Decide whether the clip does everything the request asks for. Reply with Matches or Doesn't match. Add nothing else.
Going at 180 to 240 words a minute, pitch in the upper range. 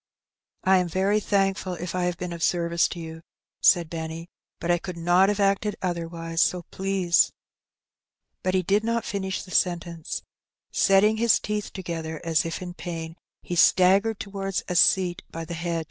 Doesn't match